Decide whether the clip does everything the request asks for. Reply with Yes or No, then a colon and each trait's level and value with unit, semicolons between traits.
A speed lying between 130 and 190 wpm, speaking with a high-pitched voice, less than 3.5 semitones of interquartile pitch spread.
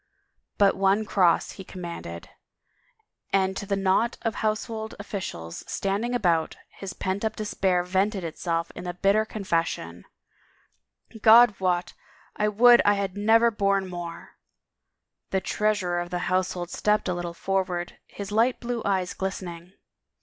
Yes: average, 155 wpm; high, 195 Hz; average, 3.0 semitones